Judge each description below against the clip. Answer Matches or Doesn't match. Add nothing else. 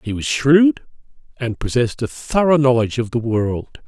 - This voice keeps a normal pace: Matches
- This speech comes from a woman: Doesn't match